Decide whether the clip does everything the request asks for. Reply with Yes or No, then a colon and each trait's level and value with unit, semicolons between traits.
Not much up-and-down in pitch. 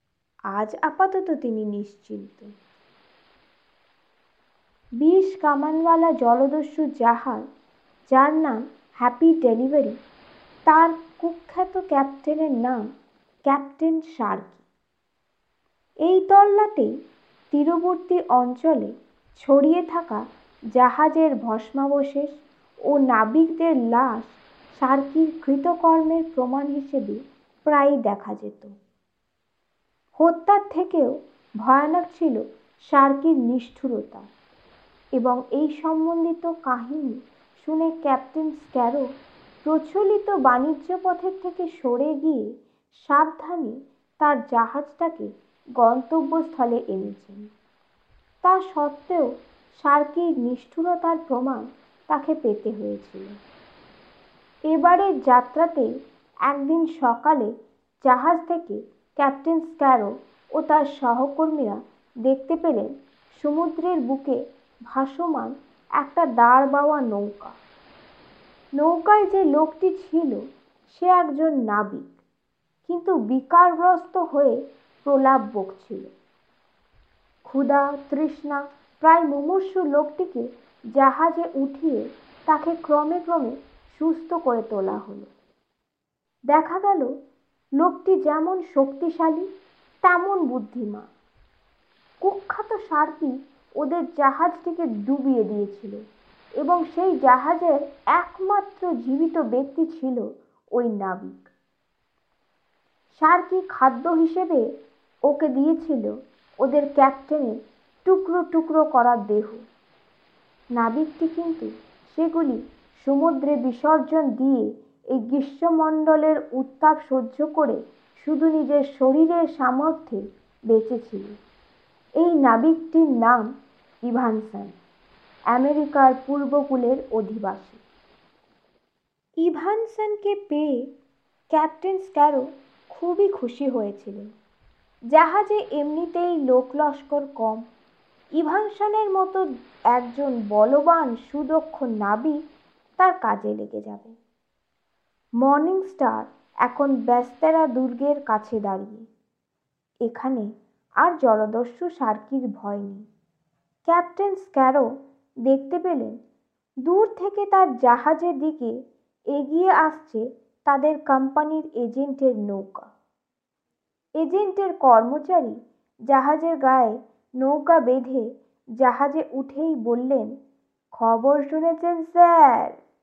No: average, 4.7 semitones